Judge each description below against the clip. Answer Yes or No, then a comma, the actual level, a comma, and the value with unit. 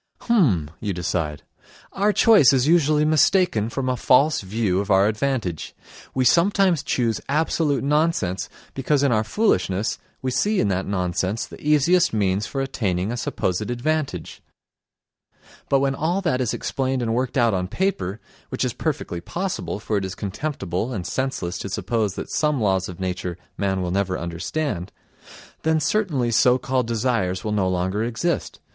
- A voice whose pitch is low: Yes, low, 115 Hz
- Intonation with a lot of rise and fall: Yes, wide, 7.4 semitones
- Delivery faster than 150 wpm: Yes, average, 165 wpm